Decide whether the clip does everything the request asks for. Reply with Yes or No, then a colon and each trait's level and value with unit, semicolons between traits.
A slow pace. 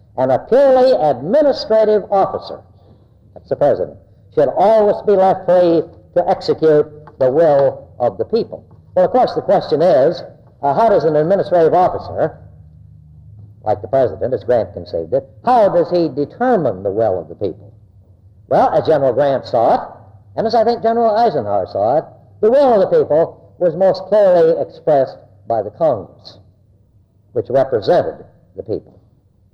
No: average, 160 wpm